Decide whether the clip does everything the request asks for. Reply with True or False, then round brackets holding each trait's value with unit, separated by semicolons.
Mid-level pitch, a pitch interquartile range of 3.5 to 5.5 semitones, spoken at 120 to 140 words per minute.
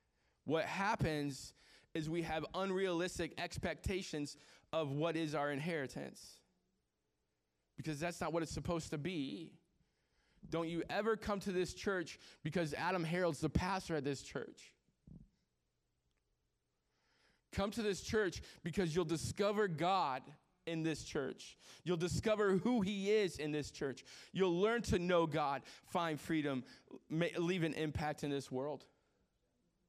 True (165 Hz; 4.0 semitones; 135 wpm)